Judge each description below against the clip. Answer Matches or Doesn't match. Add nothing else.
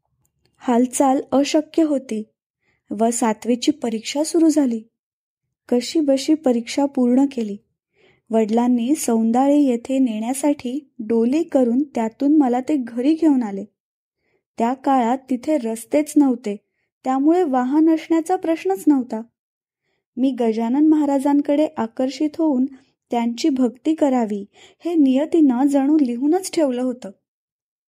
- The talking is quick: Doesn't match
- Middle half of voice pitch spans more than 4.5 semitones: Doesn't match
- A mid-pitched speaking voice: Doesn't match